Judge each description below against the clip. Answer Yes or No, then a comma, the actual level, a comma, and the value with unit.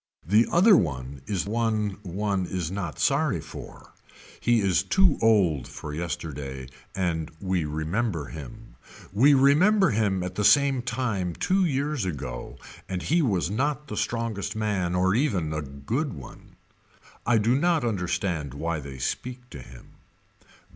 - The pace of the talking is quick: No, average, 145 wpm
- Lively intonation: Yes, wide, 6.9 semitones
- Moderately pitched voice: No, low, 100 Hz